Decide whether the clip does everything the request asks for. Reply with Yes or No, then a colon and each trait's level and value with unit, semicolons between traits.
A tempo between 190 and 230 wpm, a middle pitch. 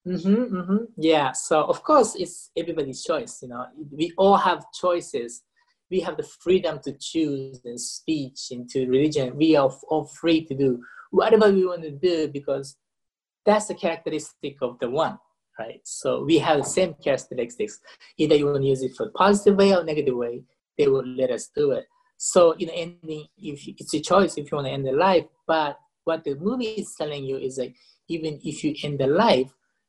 Yes: fast, 205 wpm; medium, 155 Hz